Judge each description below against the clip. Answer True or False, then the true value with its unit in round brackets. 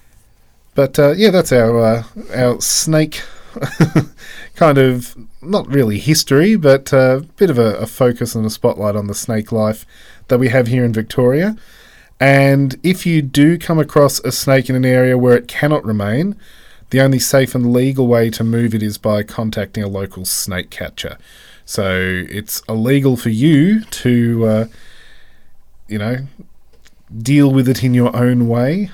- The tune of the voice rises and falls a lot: False (3.9 semitones)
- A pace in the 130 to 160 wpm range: False (170 wpm)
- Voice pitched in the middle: False (125 Hz)